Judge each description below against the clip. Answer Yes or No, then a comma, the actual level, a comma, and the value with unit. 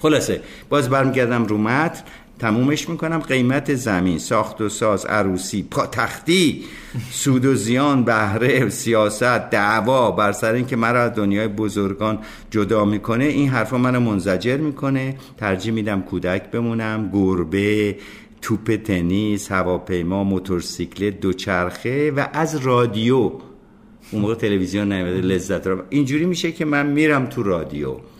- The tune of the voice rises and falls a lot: No, average, 4.7 semitones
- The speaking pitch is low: Yes, low, 110 Hz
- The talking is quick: No, average, 130 wpm